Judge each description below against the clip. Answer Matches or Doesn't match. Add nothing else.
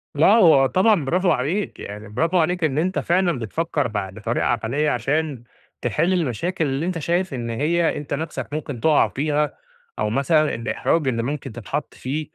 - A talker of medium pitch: Matches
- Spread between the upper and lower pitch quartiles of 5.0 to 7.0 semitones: Matches